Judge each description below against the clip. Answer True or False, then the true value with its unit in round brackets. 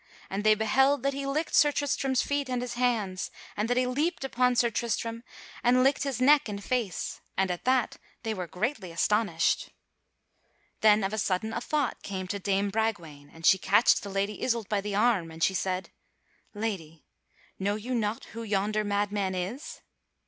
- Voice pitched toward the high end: True (215 Hz)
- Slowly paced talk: False (185 wpm)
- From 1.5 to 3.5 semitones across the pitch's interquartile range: False (4.4 semitones)